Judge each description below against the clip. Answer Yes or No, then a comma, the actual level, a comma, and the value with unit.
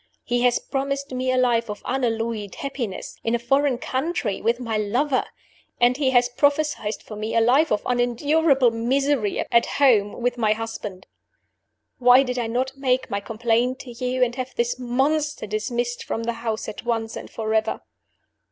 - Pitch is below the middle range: No, high, 245 Hz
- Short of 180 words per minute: Yes, average, 170 wpm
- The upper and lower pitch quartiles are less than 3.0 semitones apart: Yes, narrow, 2.6 semitones